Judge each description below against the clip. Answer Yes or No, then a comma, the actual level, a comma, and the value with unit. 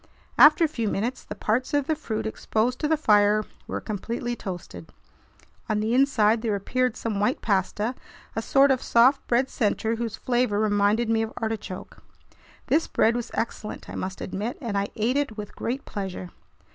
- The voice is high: Yes, high, 225 Hz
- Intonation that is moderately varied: Yes, average, 3.3 semitones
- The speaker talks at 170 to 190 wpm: Yes, average, 180 wpm